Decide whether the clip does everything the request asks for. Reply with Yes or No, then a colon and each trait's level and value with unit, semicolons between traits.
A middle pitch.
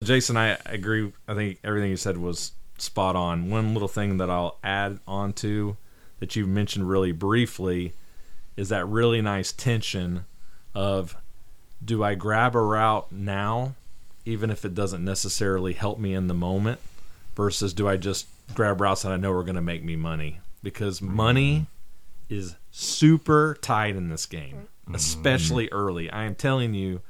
No: low, 100 Hz